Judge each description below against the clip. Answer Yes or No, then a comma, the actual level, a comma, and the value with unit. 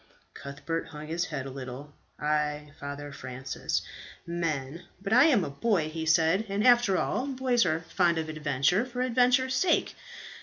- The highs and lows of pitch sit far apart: Yes, wide, 7.3 semitones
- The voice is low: No, medium, 165 Hz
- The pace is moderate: Yes, average, 160 wpm